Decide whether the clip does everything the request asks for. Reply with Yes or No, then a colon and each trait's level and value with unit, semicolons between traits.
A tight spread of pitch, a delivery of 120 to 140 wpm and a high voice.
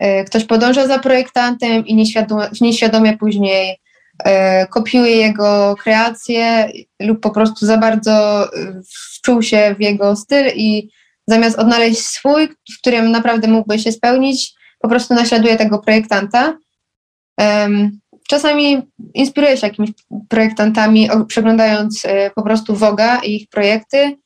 Yes: narrow, 2.1 semitones; average, 125 wpm; high, 220 Hz